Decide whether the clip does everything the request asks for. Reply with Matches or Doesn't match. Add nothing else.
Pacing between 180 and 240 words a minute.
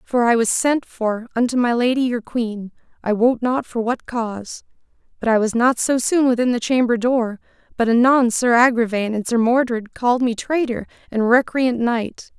Matches